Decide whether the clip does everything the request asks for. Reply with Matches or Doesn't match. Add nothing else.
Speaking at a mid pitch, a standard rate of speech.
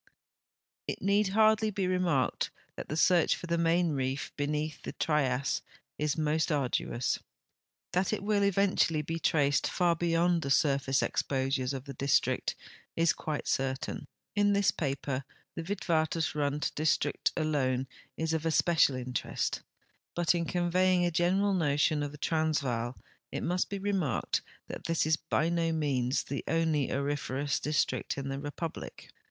Matches